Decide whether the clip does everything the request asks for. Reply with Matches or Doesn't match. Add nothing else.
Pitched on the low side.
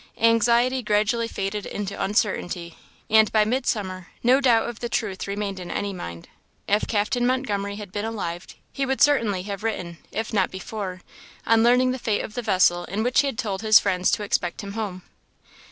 Doesn't match